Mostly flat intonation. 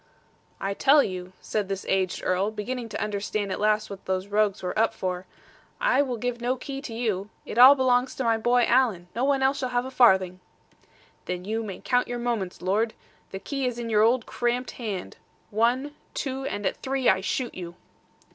No: average, 4.3 semitones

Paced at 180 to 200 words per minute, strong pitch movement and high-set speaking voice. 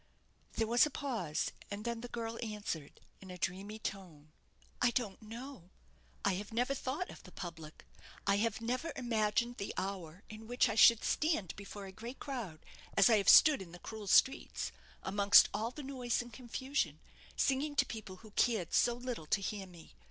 No: average, 185 wpm; average, 4.0 semitones; high, 220 Hz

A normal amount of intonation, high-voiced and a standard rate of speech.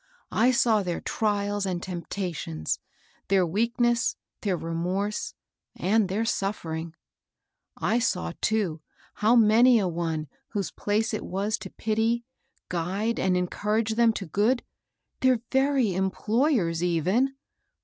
No: average, 4.2 semitones; high, 205 Hz; slow, 130 wpm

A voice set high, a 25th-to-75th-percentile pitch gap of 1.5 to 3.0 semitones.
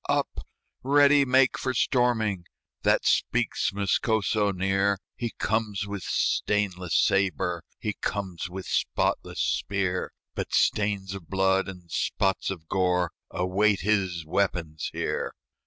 No: very low, 95 Hz; narrow, 2.5 semitones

